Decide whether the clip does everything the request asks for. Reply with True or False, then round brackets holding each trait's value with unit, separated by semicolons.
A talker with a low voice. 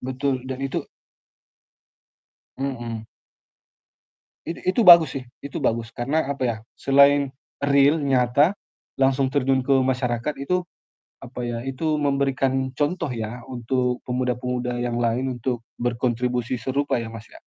True (130 Hz)